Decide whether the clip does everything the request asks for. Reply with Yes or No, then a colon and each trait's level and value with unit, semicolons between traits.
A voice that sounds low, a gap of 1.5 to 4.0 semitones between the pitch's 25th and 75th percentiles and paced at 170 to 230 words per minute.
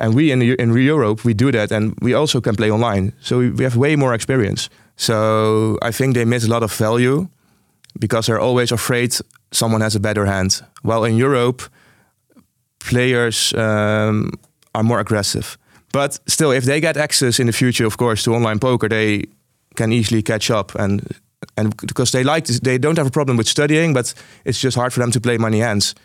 Yes: low, 120 Hz; average, 2.8 semitones; fast, 205 wpm